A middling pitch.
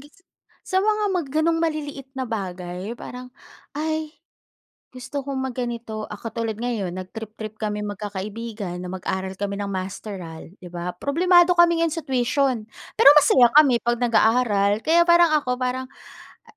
No: high, 240 Hz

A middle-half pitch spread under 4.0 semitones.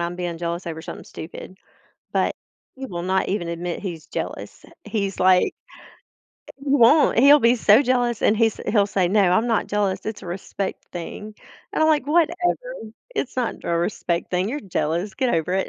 No: wide, 5.5 semitones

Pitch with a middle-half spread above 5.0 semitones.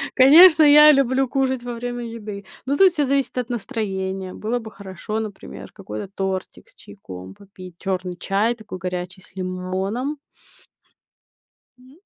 Yes: wide, 5.6 semitones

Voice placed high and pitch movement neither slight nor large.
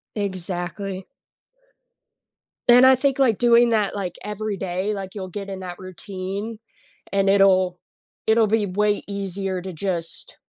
No: high, 195 Hz; narrow, 2.3 semitones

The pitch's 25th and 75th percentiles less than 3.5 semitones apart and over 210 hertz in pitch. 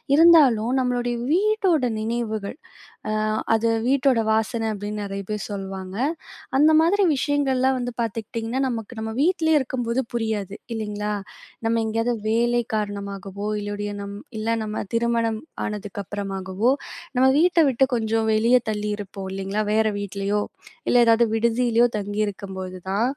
Yes: average, 3.1 semitones; high, 225 Hz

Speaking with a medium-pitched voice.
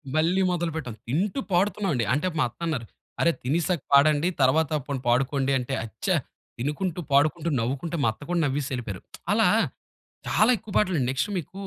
Yes: medium, 150 Hz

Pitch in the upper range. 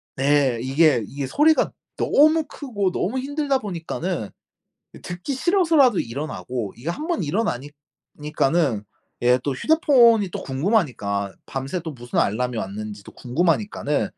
No: medium, 155 Hz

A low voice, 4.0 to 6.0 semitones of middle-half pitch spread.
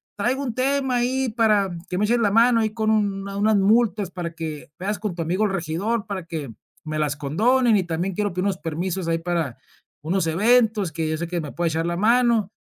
No: high, 195 Hz; average, 4.8 semitones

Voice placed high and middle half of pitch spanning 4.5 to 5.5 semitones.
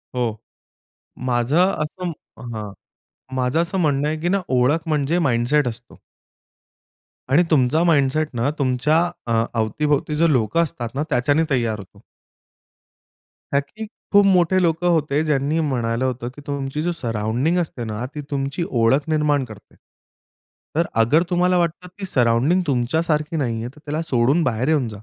No: medium, 145 Hz; average, 4.9 semitones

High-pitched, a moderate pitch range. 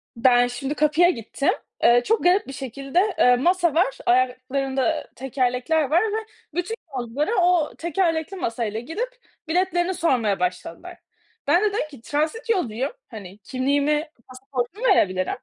No: very high, 280 Hz; wide, 6.1 semitones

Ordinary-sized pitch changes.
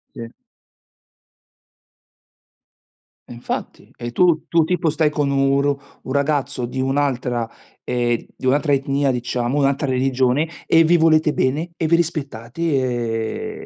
Yes: average, 3.8 semitones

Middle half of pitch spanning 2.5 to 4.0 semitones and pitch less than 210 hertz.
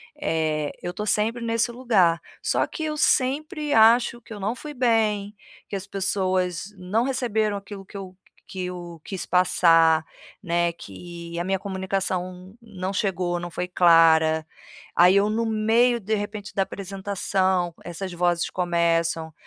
Yes: average, 3.7 semitones; high, 190 Hz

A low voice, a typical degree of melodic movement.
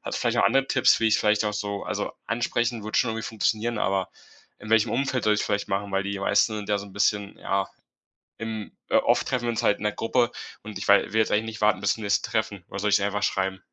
No: low, 105 Hz; narrow, 1.8 semitones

